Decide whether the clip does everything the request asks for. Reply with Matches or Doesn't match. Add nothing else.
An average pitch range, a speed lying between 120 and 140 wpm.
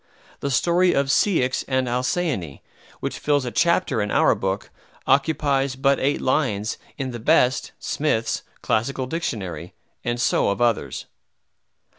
Matches